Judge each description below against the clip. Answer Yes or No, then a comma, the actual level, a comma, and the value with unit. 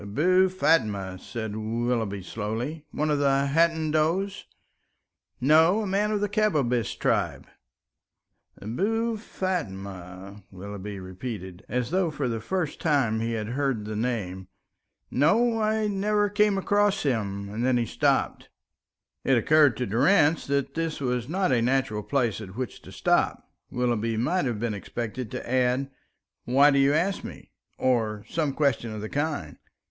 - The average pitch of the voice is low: Yes, low, 130 Hz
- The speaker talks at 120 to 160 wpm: Yes, average, 150 wpm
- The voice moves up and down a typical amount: No, wide, 7.1 semitones